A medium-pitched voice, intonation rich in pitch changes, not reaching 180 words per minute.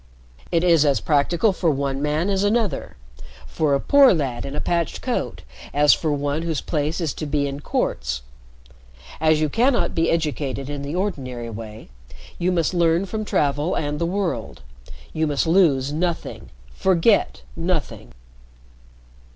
No: medium, 155 Hz; average, 3.6 semitones; average, 155 wpm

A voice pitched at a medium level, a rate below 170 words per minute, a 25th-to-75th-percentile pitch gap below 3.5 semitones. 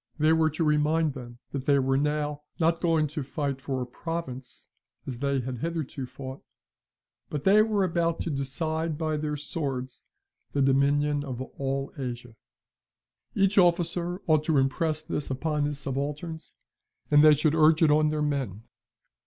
Yes: medium, 150 Hz; average, 160 wpm; average, 2.9 semitones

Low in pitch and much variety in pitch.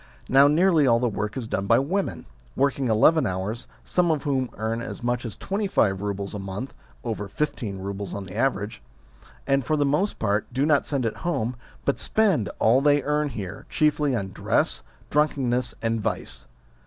Yes: low, 125 Hz; wide, 6.0 semitones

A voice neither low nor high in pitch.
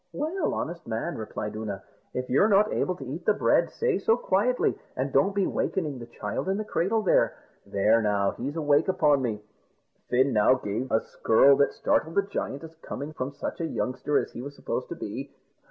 Yes: medium, 145 Hz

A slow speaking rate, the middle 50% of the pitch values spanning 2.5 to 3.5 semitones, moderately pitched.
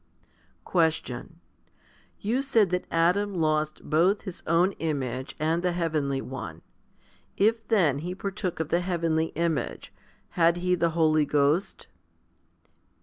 Yes: slow, 130 wpm; average, 2.9 semitones; medium, 165 Hz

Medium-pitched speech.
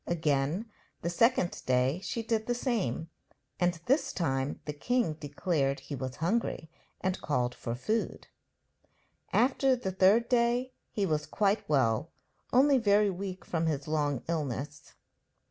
Yes: medium, 170 Hz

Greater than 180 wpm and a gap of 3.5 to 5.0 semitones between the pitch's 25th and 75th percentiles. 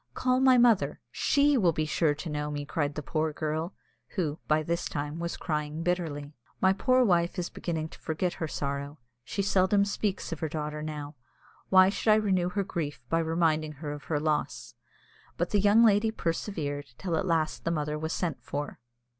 Yes: average, 195 wpm; average, 4.0 semitones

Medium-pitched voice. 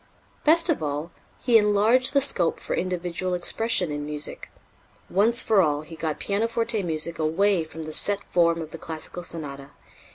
Yes: medium, 175 Hz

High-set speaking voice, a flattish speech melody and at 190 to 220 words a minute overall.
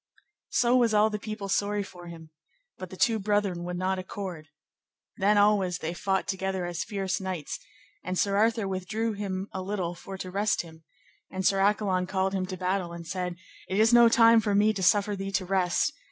Yes: high, 195 Hz; narrow, 2.2 semitones; average, 200 wpm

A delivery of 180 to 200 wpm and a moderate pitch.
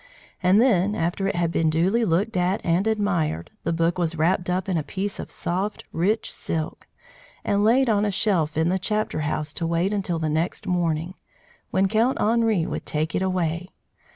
Yes: average, 190 wpm; medium, 180 Hz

